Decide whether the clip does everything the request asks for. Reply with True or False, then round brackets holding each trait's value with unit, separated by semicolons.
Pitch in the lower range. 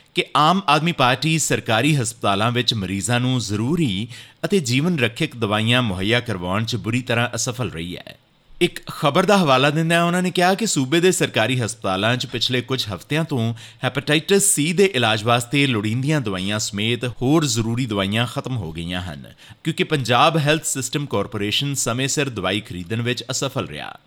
True (125 Hz)